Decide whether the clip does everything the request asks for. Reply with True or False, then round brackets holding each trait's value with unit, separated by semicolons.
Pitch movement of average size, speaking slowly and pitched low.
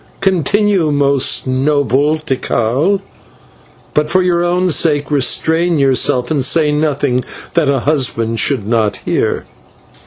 False (4.2 semitones; 120 wpm; 145 Hz)